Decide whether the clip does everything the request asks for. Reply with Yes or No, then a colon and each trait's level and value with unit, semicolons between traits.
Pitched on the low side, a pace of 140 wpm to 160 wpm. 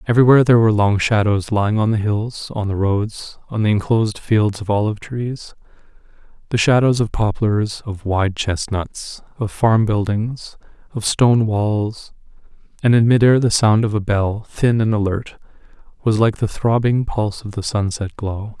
No: low, 110 Hz; average, 170 wpm